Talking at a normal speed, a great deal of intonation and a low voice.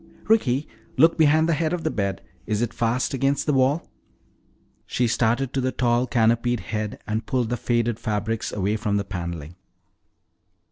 No: average, 170 wpm; average, 4.1 semitones; low, 120 Hz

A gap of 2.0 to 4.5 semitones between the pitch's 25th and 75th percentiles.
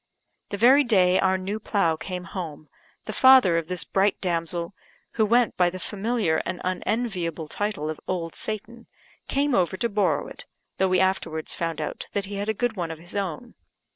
Yes: average, 4.2 semitones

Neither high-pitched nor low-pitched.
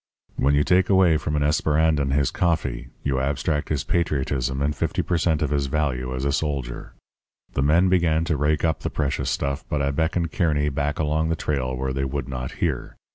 No: very low, 75 Hz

